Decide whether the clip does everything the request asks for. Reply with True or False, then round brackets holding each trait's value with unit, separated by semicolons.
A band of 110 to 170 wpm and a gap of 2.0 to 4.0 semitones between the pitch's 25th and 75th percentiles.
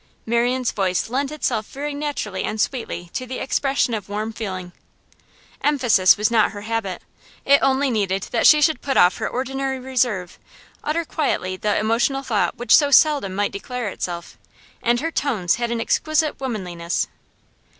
False (160 wpm; 5.0 semitones)